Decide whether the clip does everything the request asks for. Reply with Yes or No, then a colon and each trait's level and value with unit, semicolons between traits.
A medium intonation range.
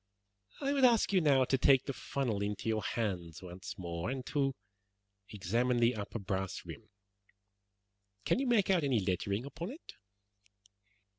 No: wide, 6.3 semitones